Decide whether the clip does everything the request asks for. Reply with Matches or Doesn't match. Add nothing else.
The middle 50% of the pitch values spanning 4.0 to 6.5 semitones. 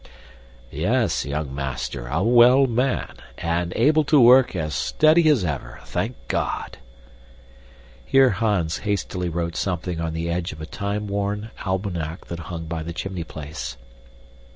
Matches